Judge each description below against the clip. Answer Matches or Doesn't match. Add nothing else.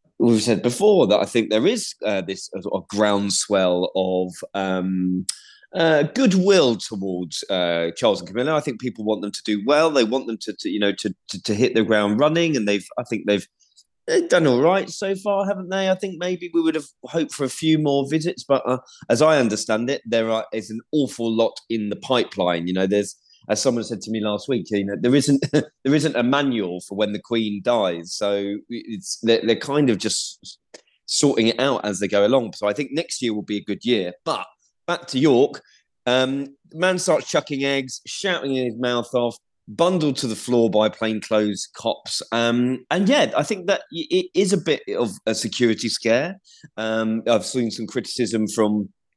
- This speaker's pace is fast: Matches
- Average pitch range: Doesn't match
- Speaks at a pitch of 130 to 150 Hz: Doesn't match